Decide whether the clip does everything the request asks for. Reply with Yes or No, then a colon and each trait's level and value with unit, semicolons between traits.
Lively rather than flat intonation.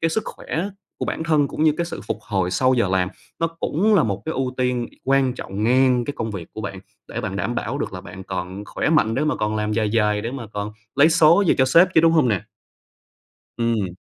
Yes: wide, 6.6 semitones